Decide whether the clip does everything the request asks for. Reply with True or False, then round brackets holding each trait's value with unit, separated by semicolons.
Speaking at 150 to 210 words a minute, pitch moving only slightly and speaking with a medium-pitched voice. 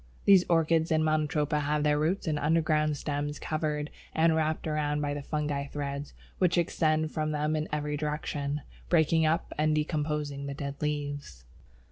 True (160 wpm; 1.2 semitones; 150 Hz)